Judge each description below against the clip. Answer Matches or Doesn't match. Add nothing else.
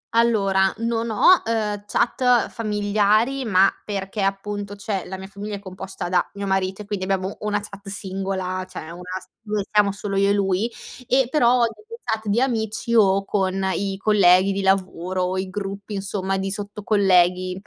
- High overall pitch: Matches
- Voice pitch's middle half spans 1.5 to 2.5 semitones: Matches